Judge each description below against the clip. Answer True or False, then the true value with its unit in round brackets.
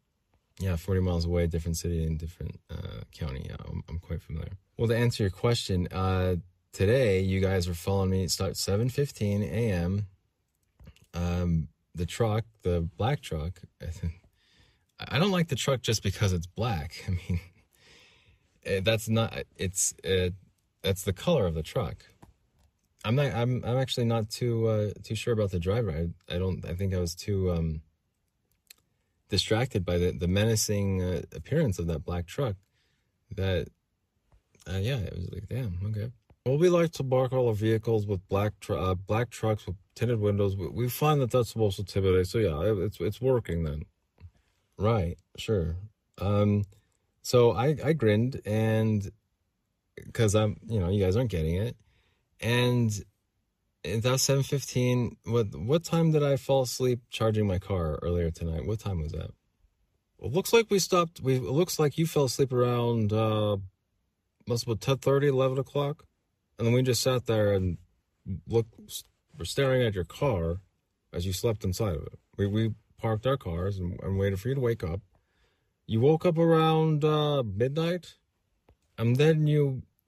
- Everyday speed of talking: True (170 wpm)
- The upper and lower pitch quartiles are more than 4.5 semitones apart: True (4.9 semitones)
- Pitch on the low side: True (105 Hz)